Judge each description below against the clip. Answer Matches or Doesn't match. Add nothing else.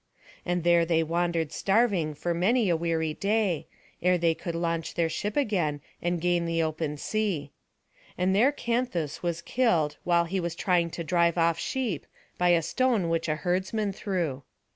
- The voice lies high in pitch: Doesn't match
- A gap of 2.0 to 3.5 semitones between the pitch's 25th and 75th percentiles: Matches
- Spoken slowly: Doesn't match